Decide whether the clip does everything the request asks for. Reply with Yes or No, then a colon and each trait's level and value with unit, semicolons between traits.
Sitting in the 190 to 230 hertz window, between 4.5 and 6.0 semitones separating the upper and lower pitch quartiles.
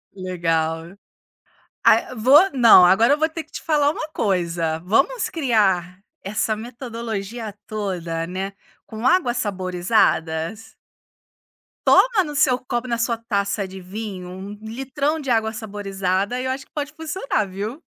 Yes: high, 220 Hz; wide, 5.5 semitones